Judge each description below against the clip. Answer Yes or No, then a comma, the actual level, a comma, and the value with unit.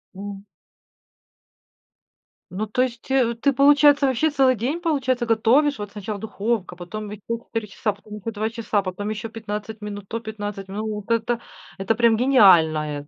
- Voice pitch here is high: Yes, high, 220 Hz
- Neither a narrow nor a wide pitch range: Yes, average, 3.0 semitones